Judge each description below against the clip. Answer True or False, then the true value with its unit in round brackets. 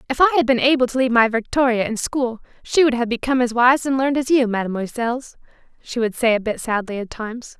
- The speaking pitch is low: False (245 Hz)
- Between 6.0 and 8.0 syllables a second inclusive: True (6.5 syllables/s)